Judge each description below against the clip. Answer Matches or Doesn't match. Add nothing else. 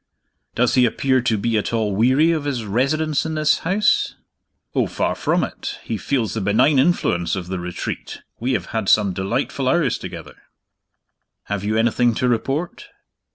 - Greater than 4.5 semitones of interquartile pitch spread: Matches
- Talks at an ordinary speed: Matches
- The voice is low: Matches